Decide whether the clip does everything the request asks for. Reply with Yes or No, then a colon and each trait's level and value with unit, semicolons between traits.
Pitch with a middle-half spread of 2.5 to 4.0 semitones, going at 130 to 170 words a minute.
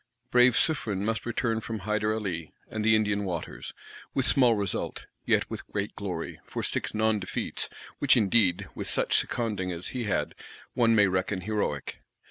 Yes: average, 3.1 semitones; average, 160 wpm